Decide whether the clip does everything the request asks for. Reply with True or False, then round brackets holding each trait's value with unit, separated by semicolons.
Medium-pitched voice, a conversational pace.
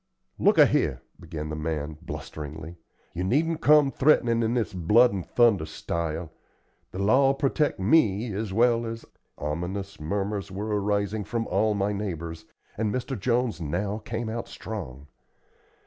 False (100 Hz; 150 wpm)